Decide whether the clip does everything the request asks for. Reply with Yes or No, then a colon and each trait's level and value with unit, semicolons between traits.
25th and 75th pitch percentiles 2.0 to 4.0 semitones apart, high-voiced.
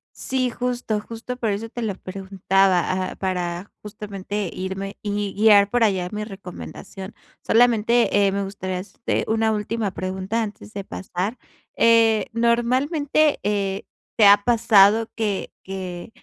Yes: average, 2.9 semitones; high, 205 Hz